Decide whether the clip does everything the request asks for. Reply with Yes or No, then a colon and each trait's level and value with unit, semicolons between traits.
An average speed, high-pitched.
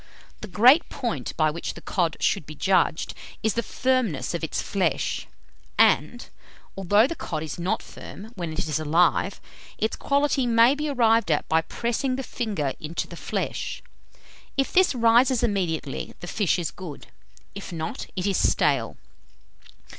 Yes: average, 160 wpm; high, 195 Hz